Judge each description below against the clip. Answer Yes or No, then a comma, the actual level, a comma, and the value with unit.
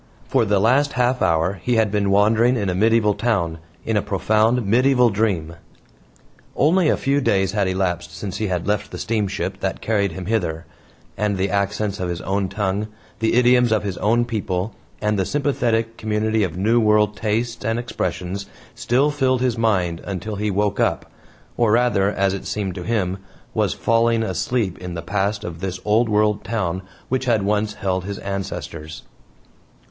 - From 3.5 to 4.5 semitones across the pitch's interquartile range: No, average, 3.1 semitones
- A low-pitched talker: Yes, low, 105 Hz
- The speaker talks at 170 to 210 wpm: Yes, average, 180 wpm